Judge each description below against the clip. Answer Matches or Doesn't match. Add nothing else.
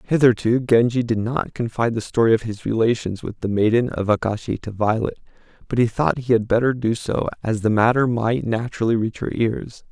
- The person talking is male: Matches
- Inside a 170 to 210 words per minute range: Matches